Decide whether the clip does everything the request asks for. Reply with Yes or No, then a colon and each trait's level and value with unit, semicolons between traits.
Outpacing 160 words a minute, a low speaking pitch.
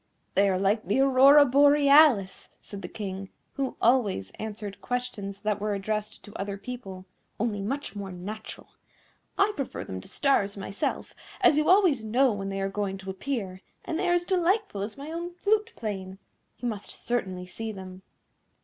No: average, 175 wpm; high, 215 Hz